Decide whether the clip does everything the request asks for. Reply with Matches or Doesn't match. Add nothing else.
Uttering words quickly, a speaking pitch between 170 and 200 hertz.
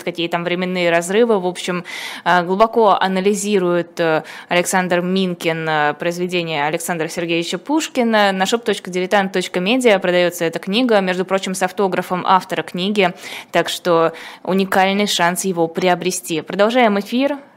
Doesn't match